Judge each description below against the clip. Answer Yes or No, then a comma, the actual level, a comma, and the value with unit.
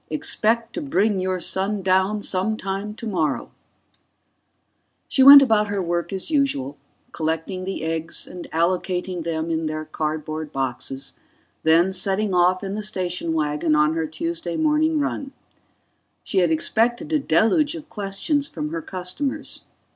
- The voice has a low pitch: No, medium, 185 Hz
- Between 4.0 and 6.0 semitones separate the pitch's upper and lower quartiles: Yes, average, 5.0 semitones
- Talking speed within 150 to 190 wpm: No, average, 140 wpm